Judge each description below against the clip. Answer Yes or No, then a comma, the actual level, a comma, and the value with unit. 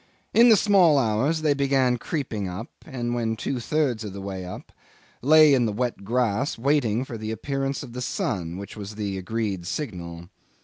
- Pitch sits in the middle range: No, low, 120 Hz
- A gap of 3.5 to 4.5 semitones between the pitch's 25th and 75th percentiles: No, average, 5.3 semitones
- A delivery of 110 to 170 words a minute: No, average, 185 wpm